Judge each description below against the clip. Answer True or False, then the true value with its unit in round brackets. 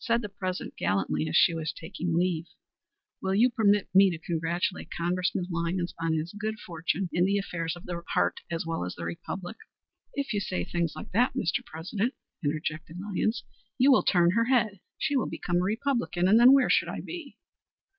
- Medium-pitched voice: True (180 Hz)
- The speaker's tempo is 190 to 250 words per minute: True (195 wpm)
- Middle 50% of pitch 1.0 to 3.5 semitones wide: False (4.3 semitones)